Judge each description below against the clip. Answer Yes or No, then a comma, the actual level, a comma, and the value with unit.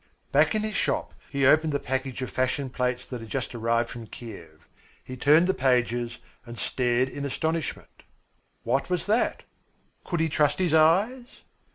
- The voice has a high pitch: No, low, 135 Hz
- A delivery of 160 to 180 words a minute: Yes, average, 170 wpm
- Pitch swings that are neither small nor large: Yes, average, 4.7 semitones